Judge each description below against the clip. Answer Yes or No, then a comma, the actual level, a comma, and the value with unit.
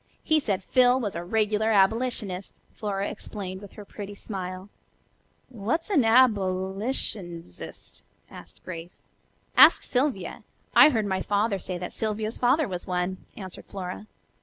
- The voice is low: No, high, 205 Hz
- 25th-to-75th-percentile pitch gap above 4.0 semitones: No, average, 3.4 semitones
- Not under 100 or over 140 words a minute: Yes, slow, 135 wpm